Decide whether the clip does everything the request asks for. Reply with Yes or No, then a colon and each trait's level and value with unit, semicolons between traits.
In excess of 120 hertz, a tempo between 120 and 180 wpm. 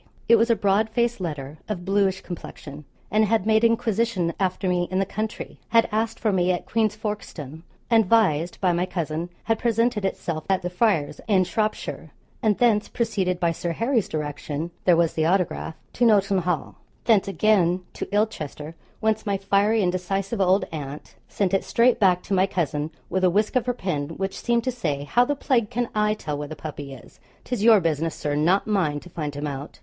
No: high, 190 Hz; average, 200 wpm